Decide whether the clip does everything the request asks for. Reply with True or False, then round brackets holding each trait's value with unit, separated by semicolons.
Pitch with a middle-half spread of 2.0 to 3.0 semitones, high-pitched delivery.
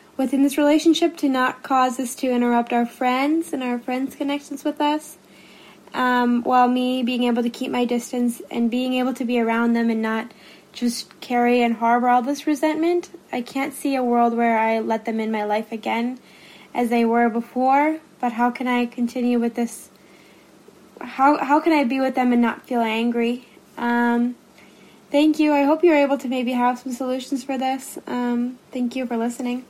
True (2.4 semitones; 250 Hz)